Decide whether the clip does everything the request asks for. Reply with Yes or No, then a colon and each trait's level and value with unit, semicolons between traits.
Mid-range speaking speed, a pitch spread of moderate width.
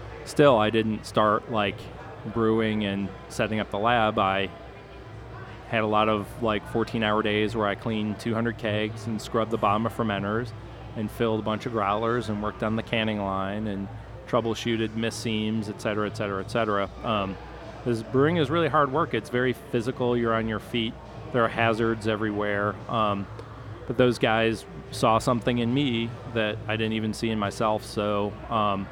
No: average, 175 wpm; narrow, 1.6 semitones